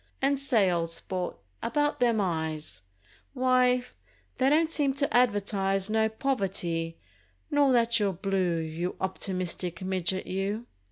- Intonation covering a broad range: Yes, wide, 5.7 semitones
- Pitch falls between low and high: No, high, 195 Hz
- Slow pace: Yes, slow, 125 wpm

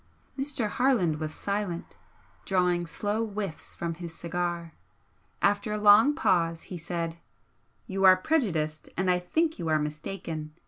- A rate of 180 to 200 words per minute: No, average, 140 wpm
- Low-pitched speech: No, medium, 180 Hz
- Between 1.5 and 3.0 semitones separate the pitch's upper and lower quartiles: No, average, 3.9 semitones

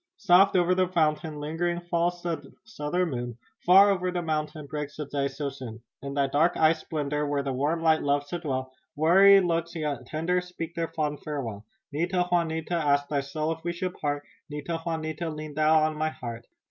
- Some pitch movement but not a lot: Yes, average, 3.1 semitones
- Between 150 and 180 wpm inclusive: No, average, 195 wpm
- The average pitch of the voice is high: No, medium, 155 Hz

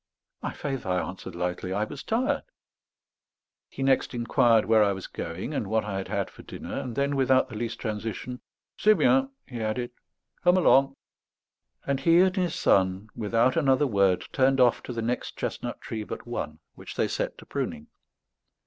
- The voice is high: No, low, 120 Hz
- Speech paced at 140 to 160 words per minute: No, average, 180 wpm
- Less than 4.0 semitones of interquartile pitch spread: No, average, 4.7 semitones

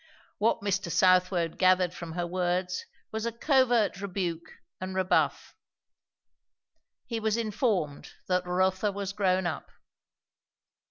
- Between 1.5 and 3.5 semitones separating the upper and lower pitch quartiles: Yes, narrow, 2.5 semitones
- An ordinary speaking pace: No, slow, 115 wpm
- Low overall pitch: No, medium, 185 Hz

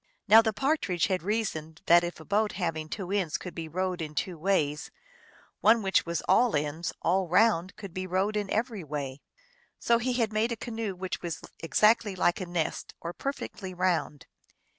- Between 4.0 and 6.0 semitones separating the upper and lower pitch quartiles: Yes, average, 4.3 semitones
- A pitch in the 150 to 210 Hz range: Yes, medium, 185 Hz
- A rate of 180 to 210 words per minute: Yes, average, 185 wpm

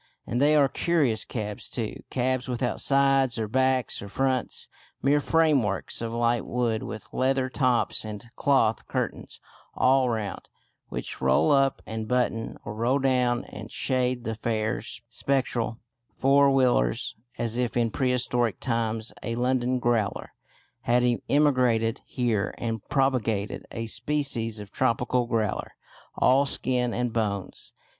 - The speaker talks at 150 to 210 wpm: No, slow, 135 wpm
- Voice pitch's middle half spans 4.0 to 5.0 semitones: No, average, 2.7 semitones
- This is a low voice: Yes, low, 120 Hz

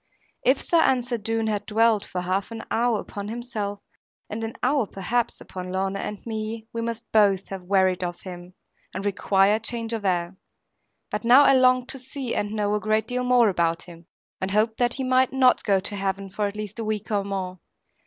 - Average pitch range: Yes, average, 3.3 semitones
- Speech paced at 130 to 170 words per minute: No, fast, 205 wpm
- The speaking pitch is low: No, high, 215 Hz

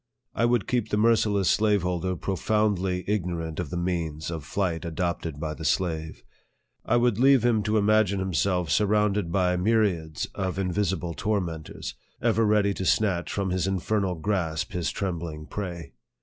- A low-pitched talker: Yes, very low, 95 Hz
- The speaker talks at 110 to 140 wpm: No, average, 165 wpm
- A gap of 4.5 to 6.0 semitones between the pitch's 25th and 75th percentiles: No, average, 3.7 semitones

